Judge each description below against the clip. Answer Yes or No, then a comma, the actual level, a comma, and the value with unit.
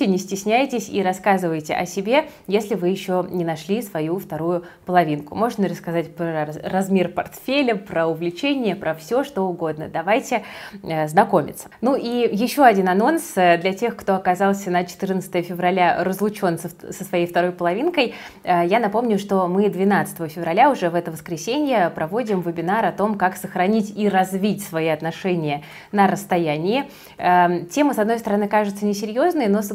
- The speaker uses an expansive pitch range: No, average, 3.5 semitones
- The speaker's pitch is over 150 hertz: Yes, high, 190 Hz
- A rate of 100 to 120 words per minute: No, average, 150 wpm